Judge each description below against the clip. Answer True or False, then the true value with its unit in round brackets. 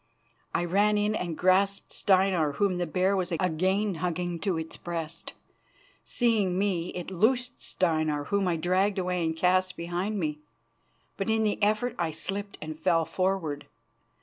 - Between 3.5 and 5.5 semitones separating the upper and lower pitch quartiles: False (3.1 semitones)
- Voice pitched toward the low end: False (185 Hz)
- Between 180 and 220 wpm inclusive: False (155 wpm)